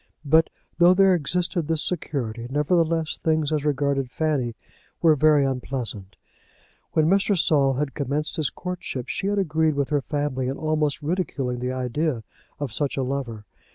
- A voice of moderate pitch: Yes, medium, 145 Hz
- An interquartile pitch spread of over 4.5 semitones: No, average, 3.3 semitones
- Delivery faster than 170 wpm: No, average, 155 wpm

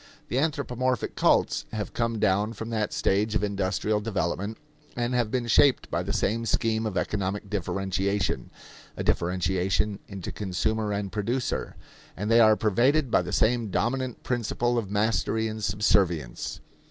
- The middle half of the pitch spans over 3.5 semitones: No, average, 2.9 semitones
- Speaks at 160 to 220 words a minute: No, average, 150 wpm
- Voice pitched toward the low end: Yes, low, 105 Hz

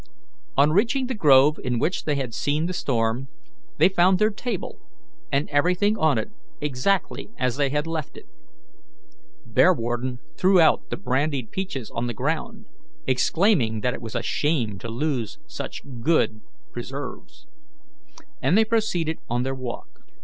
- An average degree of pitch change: No, wide, 6.6 semitones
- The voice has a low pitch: No, medium, 145 Hz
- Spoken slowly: No, average, 150 wpm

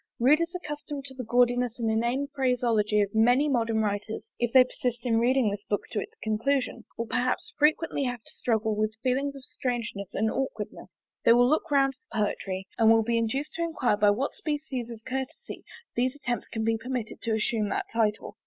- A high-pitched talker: Yes, high, 240 Hz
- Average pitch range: Yes, average, 3.3 semitones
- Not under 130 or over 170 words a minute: No, average, 195 wpm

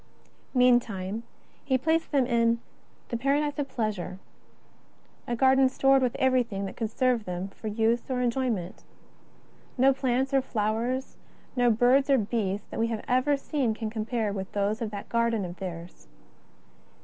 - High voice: Yes, high, 235 Hz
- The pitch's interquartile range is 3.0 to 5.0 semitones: Yes, average, 3.5 semitones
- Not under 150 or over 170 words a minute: Yes, average, 160 wpm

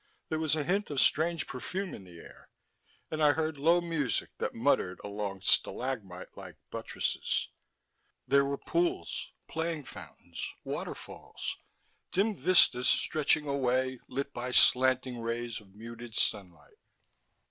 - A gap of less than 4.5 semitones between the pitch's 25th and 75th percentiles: No, average, 5.3 semitones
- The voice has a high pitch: No, low, 135 Hz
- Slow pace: Yes, slow, 130 wpm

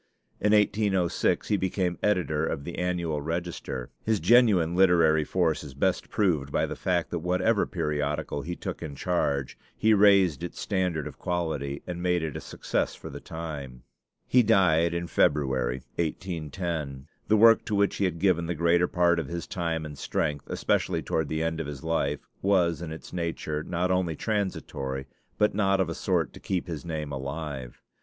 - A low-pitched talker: Yes, very low, 85 Hz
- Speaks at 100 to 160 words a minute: No, average, 180 wpm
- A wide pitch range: No, average, 3.5 semitones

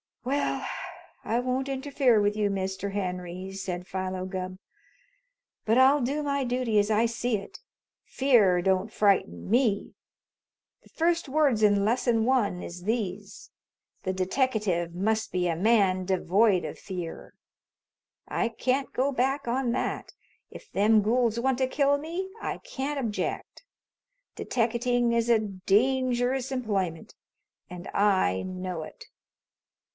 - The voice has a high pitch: Yes, high, 220 Hz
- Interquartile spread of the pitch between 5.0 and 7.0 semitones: Yes, average, 5.3 semitones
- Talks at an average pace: No, slow, 130 wpm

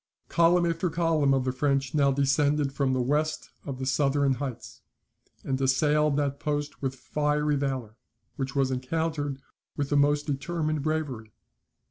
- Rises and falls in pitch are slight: Yes, narrow, 2.1 semitones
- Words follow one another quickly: No, average, 150 wpm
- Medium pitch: Yes, medium, 145 Hz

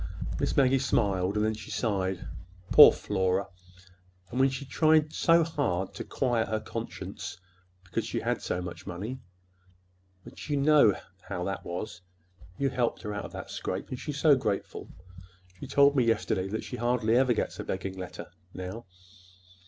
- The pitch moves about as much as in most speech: No, wide, 6.0 semitones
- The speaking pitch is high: No, low, 110 Hz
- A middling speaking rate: Yes, average, 160 wpm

